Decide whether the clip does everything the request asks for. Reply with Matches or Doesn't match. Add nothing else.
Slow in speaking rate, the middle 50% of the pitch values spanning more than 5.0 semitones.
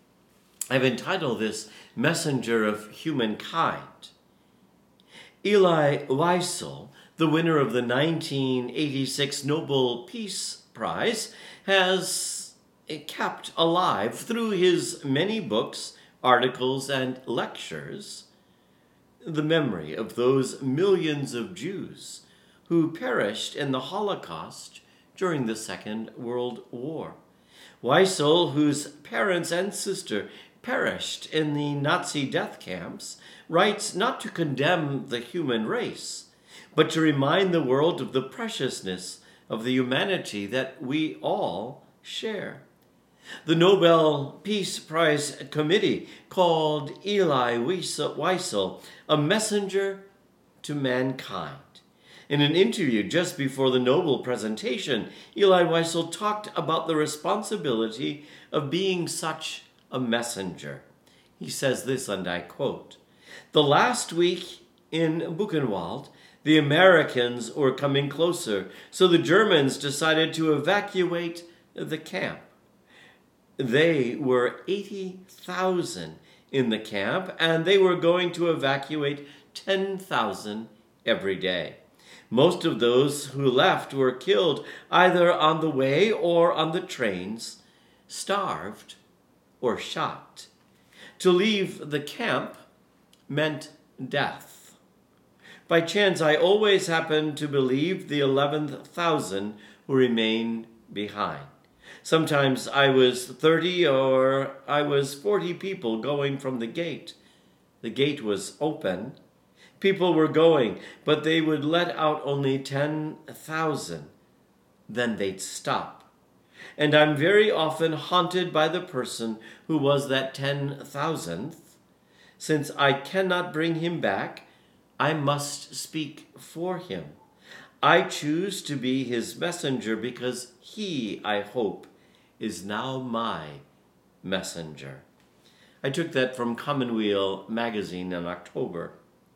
Matches